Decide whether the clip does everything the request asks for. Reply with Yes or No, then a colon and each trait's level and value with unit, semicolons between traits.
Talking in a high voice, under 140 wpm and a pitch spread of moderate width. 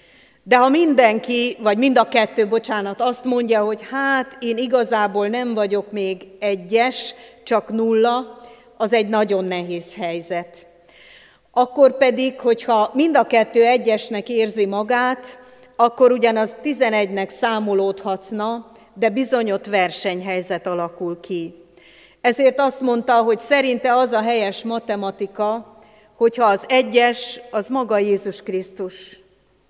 Yes: high, 225 Hz; average, 120 wpm; average, 3.6 semitones